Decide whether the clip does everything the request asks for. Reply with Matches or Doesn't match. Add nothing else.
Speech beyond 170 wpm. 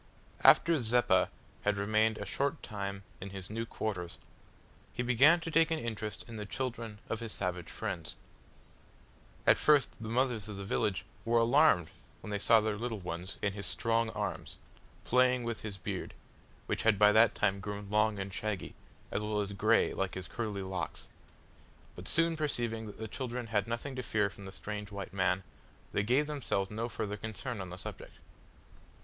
Matches